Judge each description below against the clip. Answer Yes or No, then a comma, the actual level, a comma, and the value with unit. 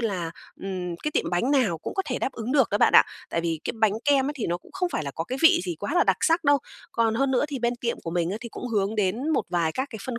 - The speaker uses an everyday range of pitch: No, wide, 7.2 semitones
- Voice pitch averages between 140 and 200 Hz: No, high, 230 Hz